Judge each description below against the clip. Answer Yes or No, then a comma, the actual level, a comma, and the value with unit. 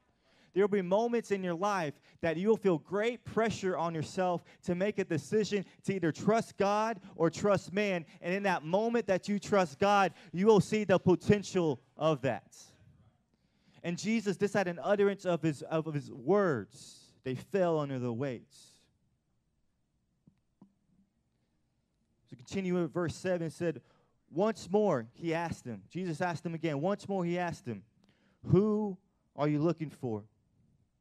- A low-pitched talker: No, medium, 180 Hz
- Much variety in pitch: No, average, 4.0 semitones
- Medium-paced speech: Yes, average, 160 wpm